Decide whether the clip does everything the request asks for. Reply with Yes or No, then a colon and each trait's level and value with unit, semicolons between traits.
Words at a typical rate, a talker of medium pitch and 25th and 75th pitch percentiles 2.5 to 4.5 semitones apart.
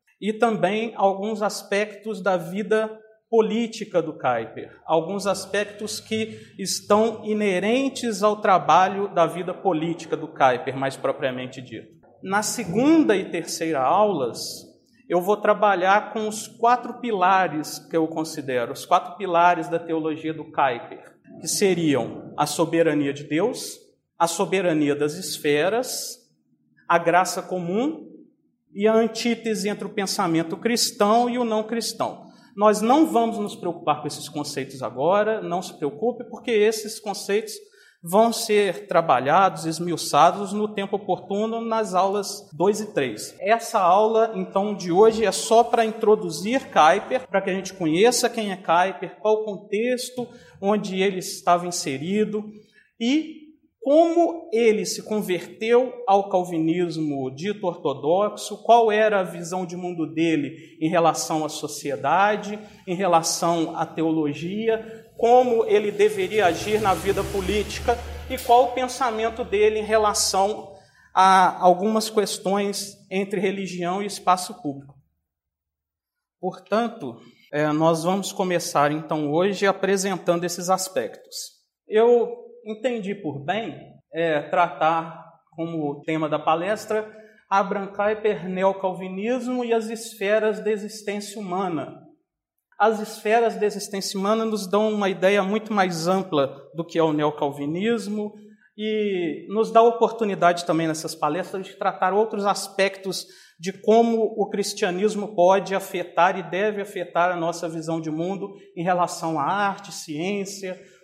No: average, 130 wpm; high, 195 Hz; average, 4.2 semitones